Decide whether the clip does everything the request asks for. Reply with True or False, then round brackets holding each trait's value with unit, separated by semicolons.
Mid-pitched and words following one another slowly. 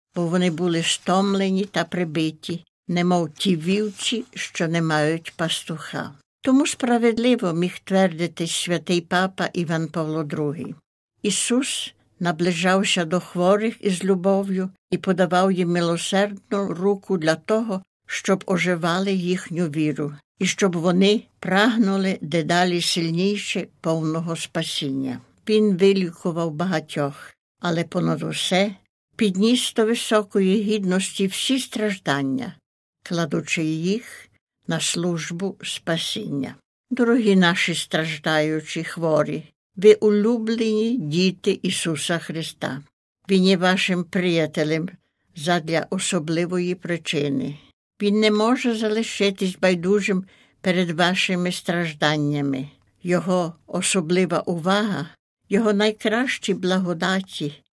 True (180 Hz; 100 wpm)